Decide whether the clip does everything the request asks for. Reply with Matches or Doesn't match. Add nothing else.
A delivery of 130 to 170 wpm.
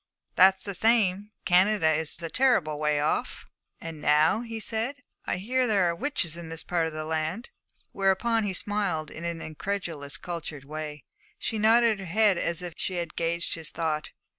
Doesn't match